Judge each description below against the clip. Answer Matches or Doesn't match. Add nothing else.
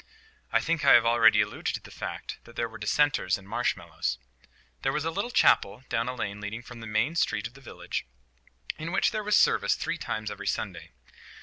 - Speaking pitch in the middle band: Doesn't match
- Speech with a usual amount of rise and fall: Doesn't match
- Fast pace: Matches